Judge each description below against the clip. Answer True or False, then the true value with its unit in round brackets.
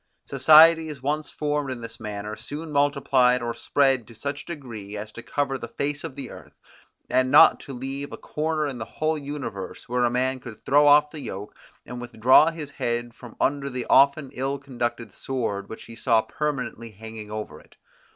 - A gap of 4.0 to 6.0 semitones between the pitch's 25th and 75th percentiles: False (3.6 semitones)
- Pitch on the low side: True (130 Hz)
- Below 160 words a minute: False (190 wpm)